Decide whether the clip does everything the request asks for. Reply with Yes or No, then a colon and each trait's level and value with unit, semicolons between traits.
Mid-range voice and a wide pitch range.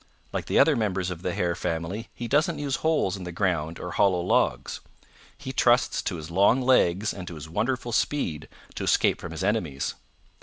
No: very low, 95 Hz; wide, 5.9 semitones